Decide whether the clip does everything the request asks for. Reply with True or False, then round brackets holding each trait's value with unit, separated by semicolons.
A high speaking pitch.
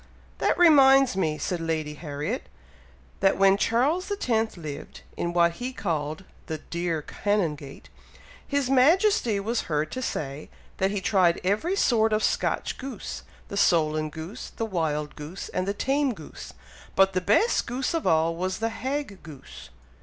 True (195 Hz)